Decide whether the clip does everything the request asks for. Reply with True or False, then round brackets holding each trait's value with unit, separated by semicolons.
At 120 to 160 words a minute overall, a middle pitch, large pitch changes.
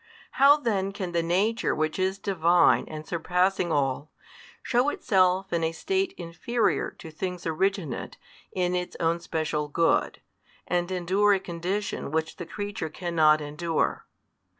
False (140 wpm; 175 Hz; 3.1 semitones)